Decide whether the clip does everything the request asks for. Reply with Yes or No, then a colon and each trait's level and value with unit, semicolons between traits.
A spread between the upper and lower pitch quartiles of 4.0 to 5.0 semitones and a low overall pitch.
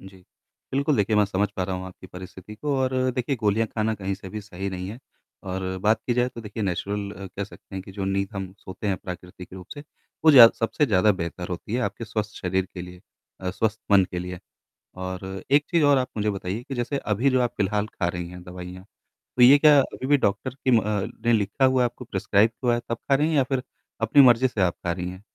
Yes: average, 4.6 semitones; low, 105 Hz